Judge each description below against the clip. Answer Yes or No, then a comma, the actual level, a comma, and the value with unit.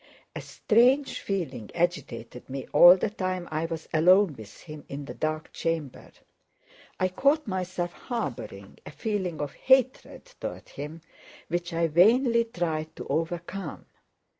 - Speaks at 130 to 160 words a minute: Yes, average, 140 wpm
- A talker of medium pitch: Yes, medium, 175 Hz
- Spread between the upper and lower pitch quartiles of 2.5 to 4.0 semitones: No, average, 4.5 semitones